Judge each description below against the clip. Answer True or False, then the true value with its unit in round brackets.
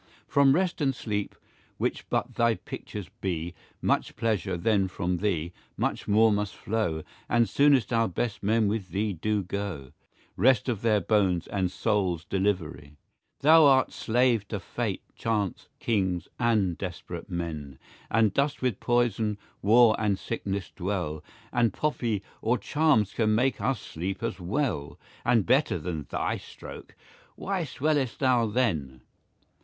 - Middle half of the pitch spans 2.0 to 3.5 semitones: False (4.6 semitones)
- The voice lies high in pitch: False (105 Hz)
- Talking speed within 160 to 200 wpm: False (150 wpm)